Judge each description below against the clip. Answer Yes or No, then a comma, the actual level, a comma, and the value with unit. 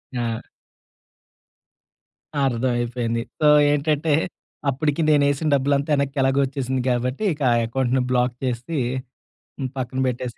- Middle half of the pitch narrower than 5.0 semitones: Yes, narrow, 2.5 semitones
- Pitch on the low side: Yes, low, 130 Hz